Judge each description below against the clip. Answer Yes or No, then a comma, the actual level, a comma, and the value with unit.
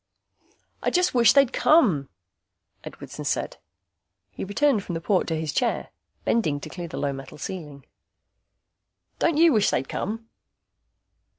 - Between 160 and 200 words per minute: No, average, 140 wpm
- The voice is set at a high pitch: Yes, high, 195 Hz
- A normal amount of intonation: No, wide, 8.8 semitones